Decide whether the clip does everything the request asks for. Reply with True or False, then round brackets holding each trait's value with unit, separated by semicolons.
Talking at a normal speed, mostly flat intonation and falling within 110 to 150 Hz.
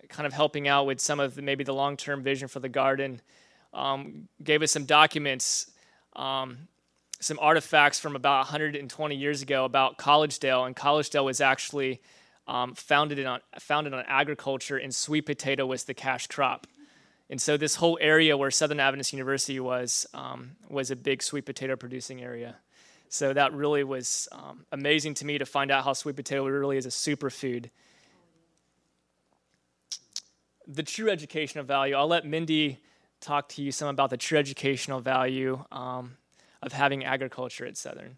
True (165 wpm; 2.0 semitones; 140 Hz)